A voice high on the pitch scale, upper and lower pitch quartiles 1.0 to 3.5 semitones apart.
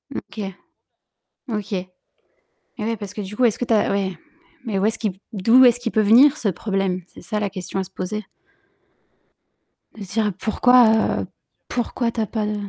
Yes: high, 210 Hz; average, 2.8 semitones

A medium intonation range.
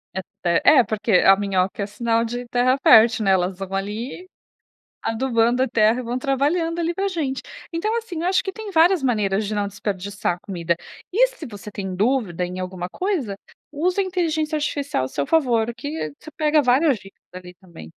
No: wide, 8.0 semitones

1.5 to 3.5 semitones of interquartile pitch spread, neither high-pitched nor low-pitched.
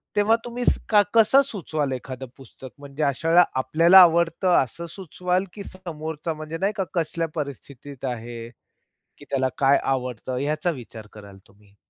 No: wide, 5.6 semitones; medium, 155 Hz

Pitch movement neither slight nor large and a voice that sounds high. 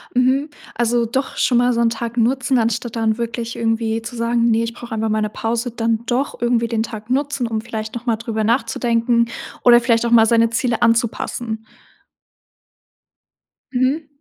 No: narrow, 1.3 semitones; high, 235 Hz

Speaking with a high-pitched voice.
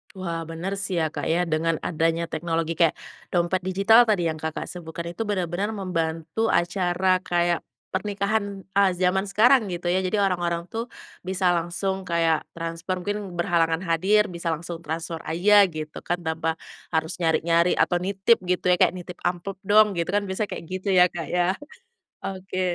No: medium, 175 Hz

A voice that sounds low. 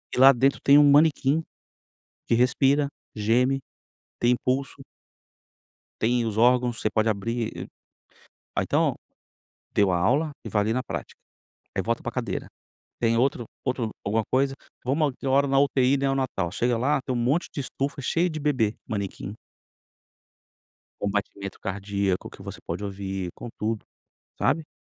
Yes: low, 125 Hz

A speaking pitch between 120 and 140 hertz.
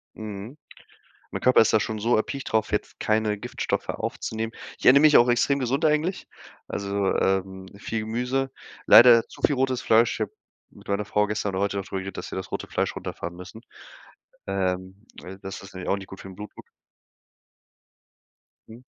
No: low, 110 Hz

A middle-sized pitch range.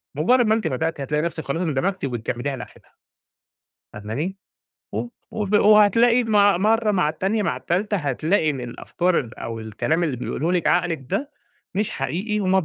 No: wide, 6.2 semitones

